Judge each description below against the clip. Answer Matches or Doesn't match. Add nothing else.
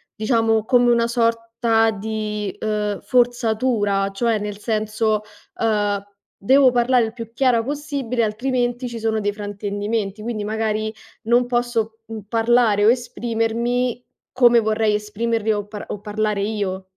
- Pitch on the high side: Matches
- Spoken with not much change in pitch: Matches